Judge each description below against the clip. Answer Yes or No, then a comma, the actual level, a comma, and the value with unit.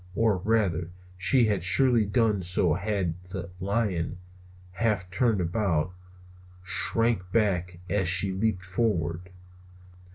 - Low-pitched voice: Yes, very low, 95 Hz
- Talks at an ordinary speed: No, slow, 120 wpm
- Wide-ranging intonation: No, average, 3.4 semitones